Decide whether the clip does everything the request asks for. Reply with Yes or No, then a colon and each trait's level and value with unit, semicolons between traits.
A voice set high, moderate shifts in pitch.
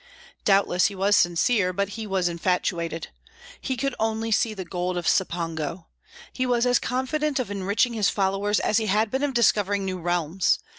Yes: high, 200 Hz; average, 4.0 semitones